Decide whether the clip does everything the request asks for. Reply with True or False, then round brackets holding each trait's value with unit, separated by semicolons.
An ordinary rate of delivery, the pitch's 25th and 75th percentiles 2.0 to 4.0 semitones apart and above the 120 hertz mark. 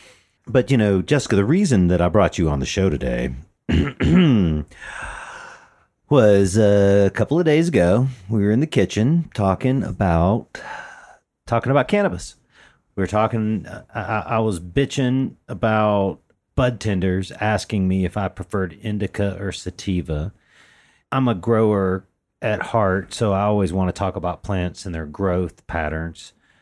False (145 wpm; 3.7 semitones; 100 Hz)